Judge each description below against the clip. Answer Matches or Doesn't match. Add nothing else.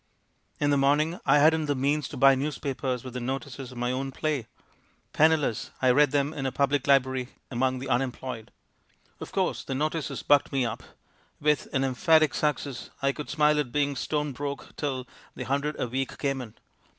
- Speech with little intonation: Matches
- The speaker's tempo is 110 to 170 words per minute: Doesn't match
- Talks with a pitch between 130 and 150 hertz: Matches